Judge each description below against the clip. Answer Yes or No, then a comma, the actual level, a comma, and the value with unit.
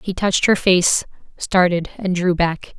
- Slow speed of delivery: No, average, 170 wpm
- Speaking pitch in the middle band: Yes, medium, 180 Hz